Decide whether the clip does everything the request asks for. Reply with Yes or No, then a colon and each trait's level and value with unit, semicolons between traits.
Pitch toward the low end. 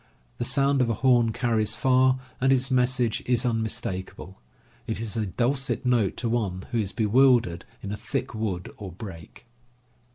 Yes: low, 115 Hz